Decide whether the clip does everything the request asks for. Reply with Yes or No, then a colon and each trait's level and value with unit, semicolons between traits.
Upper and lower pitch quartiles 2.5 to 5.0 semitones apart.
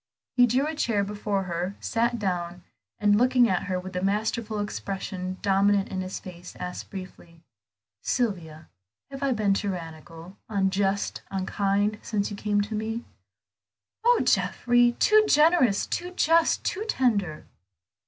Yes: average, 4.1 semitones